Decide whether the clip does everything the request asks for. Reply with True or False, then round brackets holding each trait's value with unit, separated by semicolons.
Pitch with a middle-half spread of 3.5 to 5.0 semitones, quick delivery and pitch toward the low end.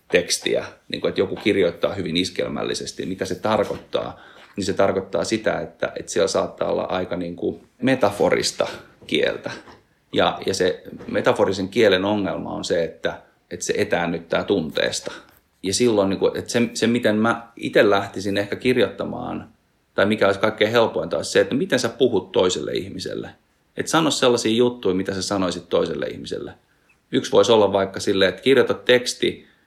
True (4.3 semitones; 165 wpm; 100 Hz)